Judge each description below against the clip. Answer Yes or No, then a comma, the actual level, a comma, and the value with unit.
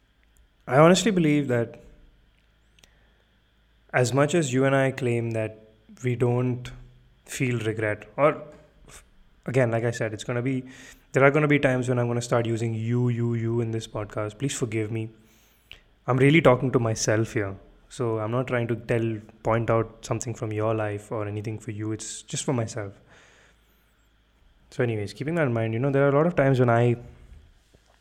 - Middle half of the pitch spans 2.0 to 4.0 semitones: Yes, average, 3.1 semitones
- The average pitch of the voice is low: Yes, low, 120 Hz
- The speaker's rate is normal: Yes, average, 190 wpm